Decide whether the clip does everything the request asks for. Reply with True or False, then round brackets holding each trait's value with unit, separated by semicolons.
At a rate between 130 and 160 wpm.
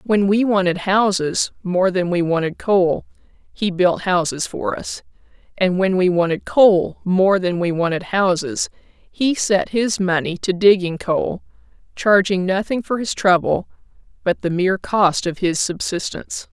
True (155 wpm)